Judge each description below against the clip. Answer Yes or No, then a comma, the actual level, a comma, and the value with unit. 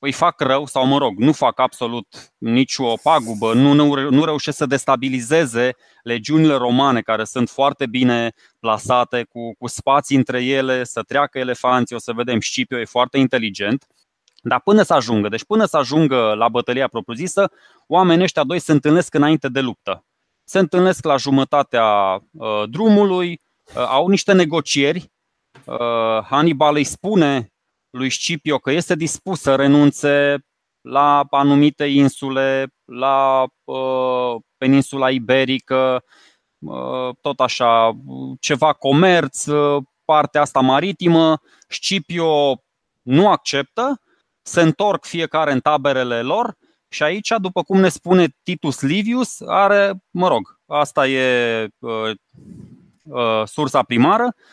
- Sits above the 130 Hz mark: Yes, medium, 140 Hz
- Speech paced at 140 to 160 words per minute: No, average, 130 wpm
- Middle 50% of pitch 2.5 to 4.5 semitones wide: Yes, average, 4.1 semitones